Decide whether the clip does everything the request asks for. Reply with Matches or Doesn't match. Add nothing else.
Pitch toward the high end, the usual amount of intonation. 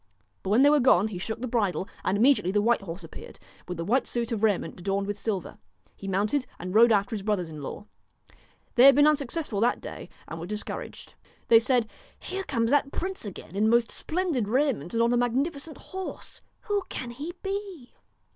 Doesn't match